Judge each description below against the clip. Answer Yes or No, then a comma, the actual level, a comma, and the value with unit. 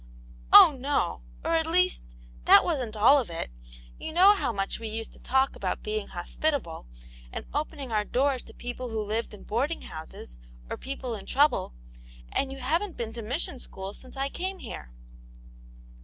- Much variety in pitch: Yes, wide, 5.7 semitones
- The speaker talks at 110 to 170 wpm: No, average, 185 wpm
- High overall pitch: Yes, very high, 255 Hz